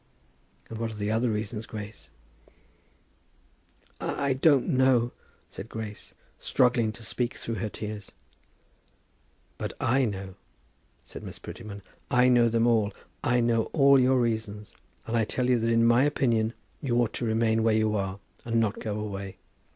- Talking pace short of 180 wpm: Yes, average, 160 wpm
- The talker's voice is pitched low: Yes, low, 115 Hz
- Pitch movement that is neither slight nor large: No, narrow, 2.2 semitones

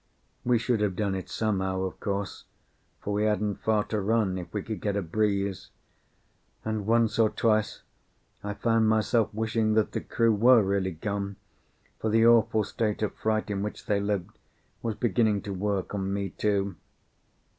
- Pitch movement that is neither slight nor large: No, narrow, 1.8 semitones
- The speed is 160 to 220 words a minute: Yes, average, 175 wpm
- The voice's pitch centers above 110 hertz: No, low, 105 Hz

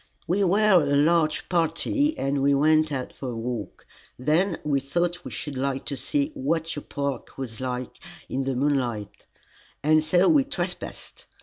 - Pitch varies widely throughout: No, average, 4.4 semitones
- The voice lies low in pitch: No, medium, 150 Hz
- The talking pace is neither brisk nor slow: Yes, average, 170 wpm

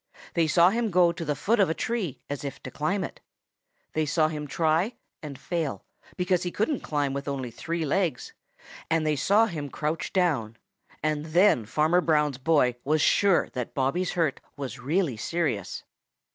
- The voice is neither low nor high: Yes, medium, 155 Hz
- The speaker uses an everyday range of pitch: Yes, average, 4.0 semitones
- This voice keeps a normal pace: Yes, average, 175 wpm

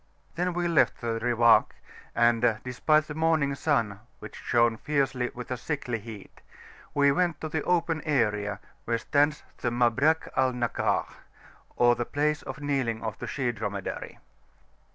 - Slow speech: No, average, 155 wpm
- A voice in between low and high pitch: No, low, 125 Hz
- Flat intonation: No, average, 4.4 semitones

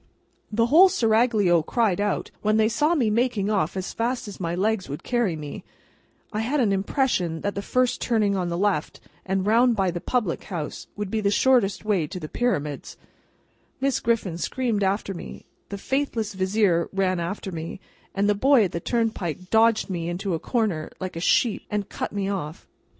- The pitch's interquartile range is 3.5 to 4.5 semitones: Yes, average, 4.0 semitones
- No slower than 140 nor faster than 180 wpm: No, average, 190 wpm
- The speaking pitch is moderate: No, high, 205 Hz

